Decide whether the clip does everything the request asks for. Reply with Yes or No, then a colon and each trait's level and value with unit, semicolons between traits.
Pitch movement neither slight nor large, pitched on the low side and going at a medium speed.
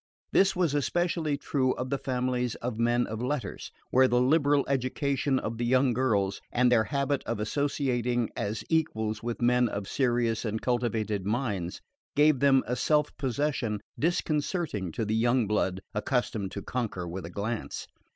Yes: average, 4.0 semitones; low, 125 Hz; average, 160 wpm